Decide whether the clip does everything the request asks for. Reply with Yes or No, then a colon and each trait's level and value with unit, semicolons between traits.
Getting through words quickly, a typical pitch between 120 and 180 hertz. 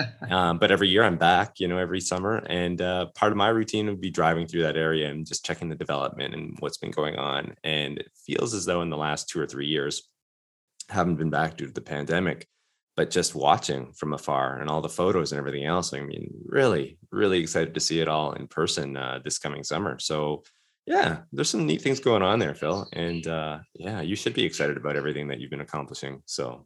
No: fast, 230 wpm; very low, 80 Hz